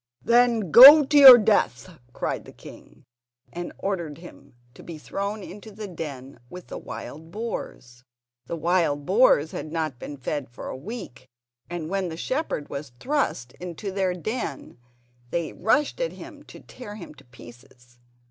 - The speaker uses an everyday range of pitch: No, wide, 6.9 semitones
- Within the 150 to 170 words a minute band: Yes, average, 160 wpm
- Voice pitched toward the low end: No, medium, 175 Hz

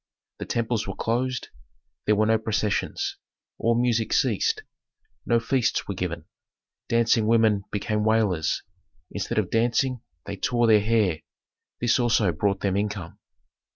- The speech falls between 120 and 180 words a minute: Yes, slow, 135 wpm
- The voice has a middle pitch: No, low, 110 Hz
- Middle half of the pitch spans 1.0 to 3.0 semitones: Yes, narrow, 2.5 semitones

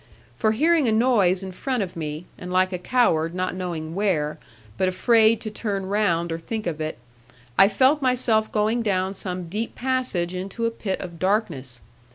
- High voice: Yes, high, 195 Hz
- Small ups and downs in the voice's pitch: No, average, 4.3 semitones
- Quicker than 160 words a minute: Yes, average, 185 wpm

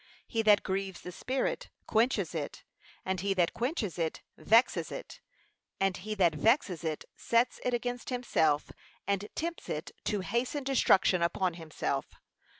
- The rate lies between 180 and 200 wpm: No, average, 150 wpm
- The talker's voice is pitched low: No, high, 200 Hz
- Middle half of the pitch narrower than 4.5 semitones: No, wide, 5.4 semitones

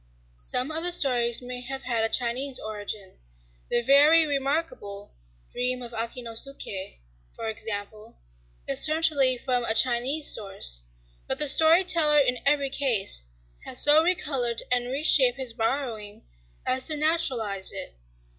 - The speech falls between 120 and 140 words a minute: Yes, slow, 135 wpm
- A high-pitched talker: Yes, very high, 250 Hz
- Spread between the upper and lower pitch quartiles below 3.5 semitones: No, average, 4.2 semitones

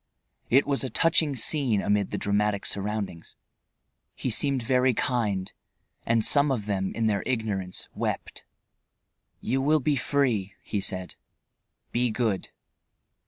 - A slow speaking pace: Yes, slow, 130 wpm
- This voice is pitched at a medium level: No, low, 115 Hz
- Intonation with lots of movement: No, average, 4.7 semitones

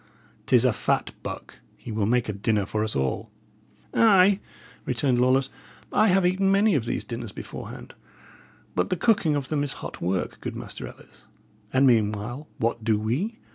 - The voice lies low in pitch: Yes, low, 125 Hz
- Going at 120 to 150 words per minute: No, average, 175 wpm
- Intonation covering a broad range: Yes, wide, 8.6 semitones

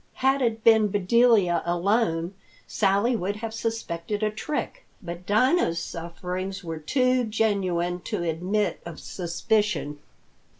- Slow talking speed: Yes, slow, 120 wpm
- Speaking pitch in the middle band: No, high, 200 Hz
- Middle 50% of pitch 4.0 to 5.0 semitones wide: Yes, average, 4.5 semitones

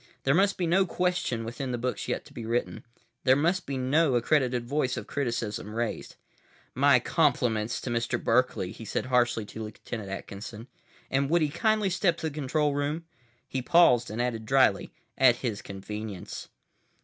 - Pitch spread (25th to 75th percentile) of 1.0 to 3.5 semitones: No, average, 4.9 semitones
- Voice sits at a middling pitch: No, low, 125 Hz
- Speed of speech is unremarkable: Yes, average, 175 wpm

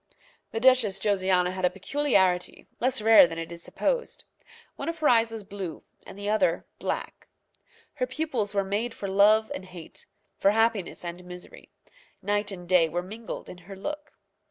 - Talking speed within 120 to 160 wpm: No, average, 175 wpm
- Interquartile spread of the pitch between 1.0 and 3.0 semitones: No, average, 3.8 semitones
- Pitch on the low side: No, high, 200 Hz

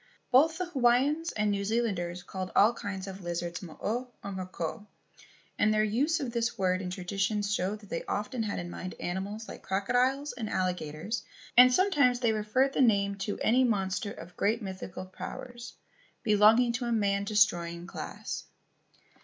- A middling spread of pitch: Yes, average, 4.3 semitones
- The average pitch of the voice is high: Yes, high, 210 Hz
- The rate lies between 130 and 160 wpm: No, average, 170 wpm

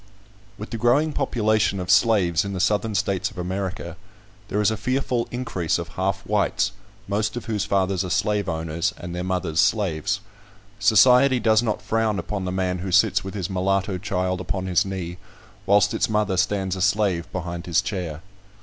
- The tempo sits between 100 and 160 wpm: No, average, 175 wpm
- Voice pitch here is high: No, very low, 95 Hz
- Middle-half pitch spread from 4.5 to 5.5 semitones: No, average, 2.7 semitones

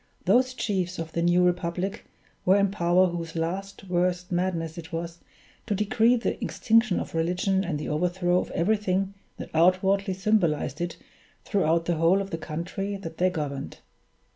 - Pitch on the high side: No, medium, 180 Hz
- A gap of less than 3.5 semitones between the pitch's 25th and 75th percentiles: Yes, average, 2.7 semitones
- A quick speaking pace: No, average, 165 wpm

